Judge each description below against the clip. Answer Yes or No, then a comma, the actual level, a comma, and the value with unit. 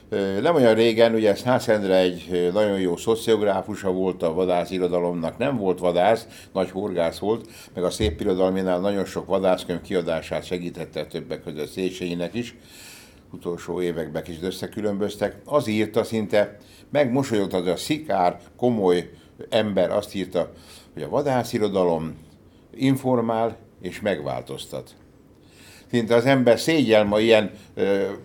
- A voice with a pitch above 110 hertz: No, very low, 95 Hz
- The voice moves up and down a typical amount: Yes, average, 4.1 semitones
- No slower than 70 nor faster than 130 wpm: Yes, average, 125 wpm